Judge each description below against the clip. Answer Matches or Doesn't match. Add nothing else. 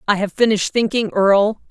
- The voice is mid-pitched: Doesn't match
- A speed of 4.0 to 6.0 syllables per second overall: Doesn't match